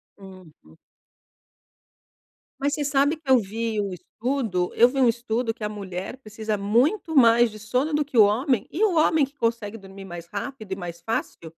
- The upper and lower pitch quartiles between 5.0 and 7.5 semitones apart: Yes, average, 5.3 semitones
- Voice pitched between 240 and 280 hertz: No, high, 225 Hz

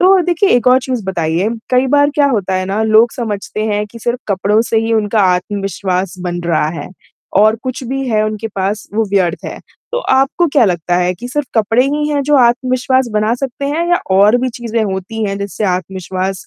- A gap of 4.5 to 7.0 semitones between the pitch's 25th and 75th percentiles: Yes, average, 5.0 semitones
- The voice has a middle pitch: No, high, 220 Hz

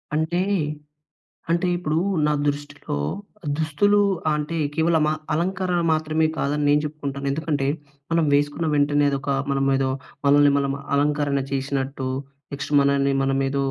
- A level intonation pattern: Yes, narrow, 2.2 semitones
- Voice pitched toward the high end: No, medium, 145 Hz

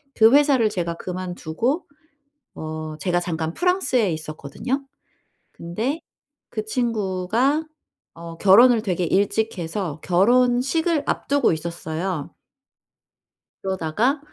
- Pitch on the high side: Yes, high, 195 Hz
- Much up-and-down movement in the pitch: Yes, wide, 6.8 semitones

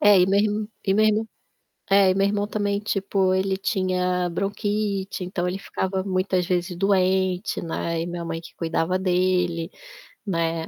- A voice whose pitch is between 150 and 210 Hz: Yes, high, 190 Hz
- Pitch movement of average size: No, narrow, 1.9 semitones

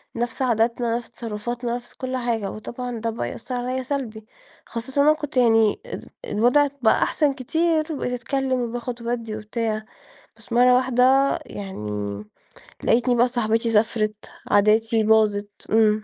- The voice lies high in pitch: Yes, high, 235 Hz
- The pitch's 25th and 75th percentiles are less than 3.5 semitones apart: Yes, narrow, 2.5 semitones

